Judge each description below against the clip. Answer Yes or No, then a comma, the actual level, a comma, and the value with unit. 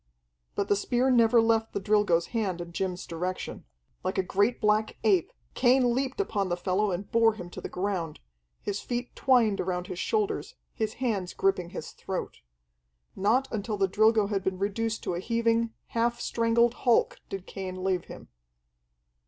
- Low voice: No, high, 210 Hz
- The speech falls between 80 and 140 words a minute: No, average, 170 wpm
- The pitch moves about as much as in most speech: Yes, average, 3.6 semitones